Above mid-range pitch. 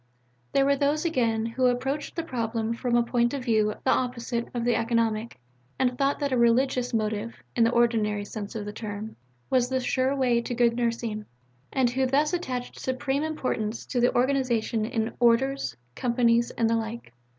Yes: high, 240 Hz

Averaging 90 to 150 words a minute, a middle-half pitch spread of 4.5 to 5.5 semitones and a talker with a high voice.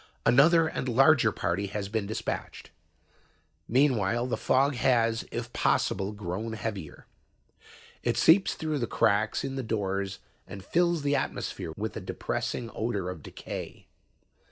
No: slow, 135 wpm; average, 5.2 semitones; low, 115 Hz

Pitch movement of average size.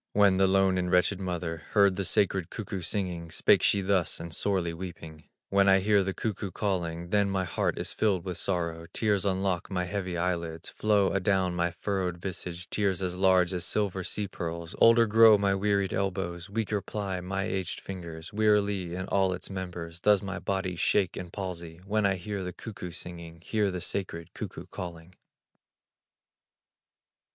No: narrow, 2.3 semitones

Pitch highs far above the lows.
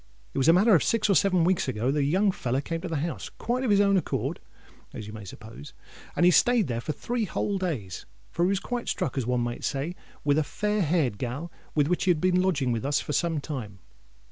Yes: wide, 6.3 semitones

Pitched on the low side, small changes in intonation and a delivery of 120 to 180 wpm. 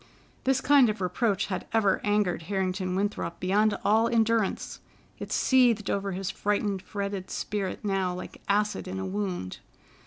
No: high, 200 Hz; narrow, 2.1 semitones; average, 150 wpm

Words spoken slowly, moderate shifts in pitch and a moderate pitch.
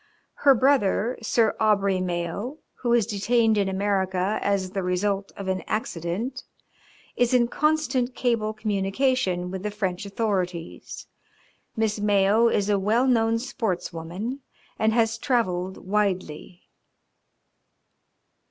No: slow, 120 wpm; average, 3.6 semitones; high, 210 Hz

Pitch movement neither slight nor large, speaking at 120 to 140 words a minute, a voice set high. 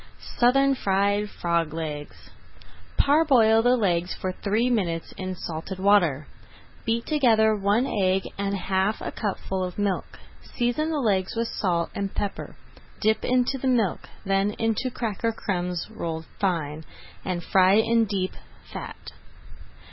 Yes: average, 3.8 semitones; slow, 135 wpm; high, 200 Hz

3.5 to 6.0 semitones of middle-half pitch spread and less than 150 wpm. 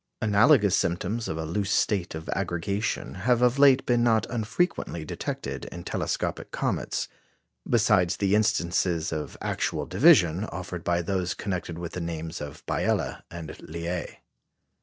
Yes: average, 4.3 semitones; average, 140 wpm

